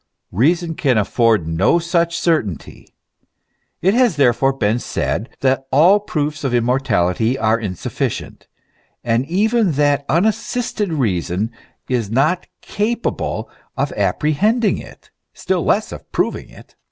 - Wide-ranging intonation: Yes, wide, 7.1 semitones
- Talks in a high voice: No, medium, 140 Hz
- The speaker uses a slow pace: Yes, slow, 120 wpm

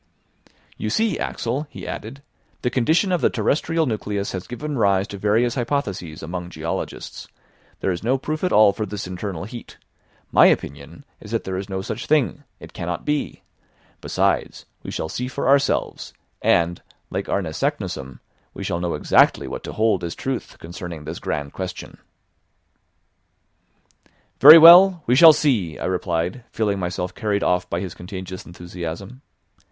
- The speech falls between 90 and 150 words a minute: No, average, 160 wpm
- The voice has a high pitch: No, low, 100 Hz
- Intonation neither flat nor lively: No, wide, 6.9 semitones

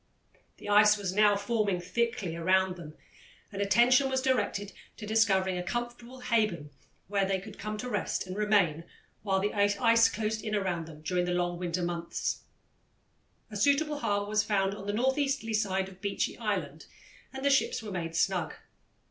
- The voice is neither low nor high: No, high, 205 Hz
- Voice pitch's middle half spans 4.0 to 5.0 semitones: No, average, 3.3 semitones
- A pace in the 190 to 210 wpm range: No, average, 175 wpm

